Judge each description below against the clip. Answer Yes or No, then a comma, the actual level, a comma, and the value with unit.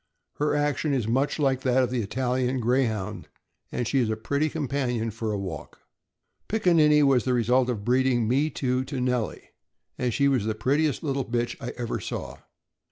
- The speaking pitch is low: Yes, low, 125 Hz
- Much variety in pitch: No, average, 2.9 semitones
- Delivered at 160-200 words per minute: Yes, average, 185 wpm